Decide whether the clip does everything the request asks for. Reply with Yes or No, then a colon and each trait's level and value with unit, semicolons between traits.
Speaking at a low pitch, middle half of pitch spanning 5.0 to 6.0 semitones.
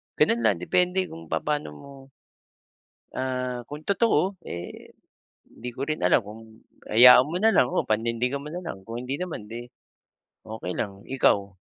Yes: low, 125 Hz; wide, 5.5 semitones